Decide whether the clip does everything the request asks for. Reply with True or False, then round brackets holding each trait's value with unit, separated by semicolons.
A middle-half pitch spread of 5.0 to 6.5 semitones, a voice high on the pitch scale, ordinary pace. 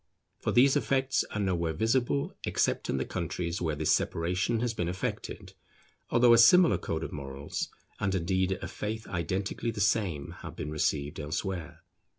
False (5.6 semitones; 95 Hz; 160 wpm)